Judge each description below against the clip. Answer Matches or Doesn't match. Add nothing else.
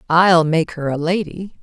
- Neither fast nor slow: Matches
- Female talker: Matches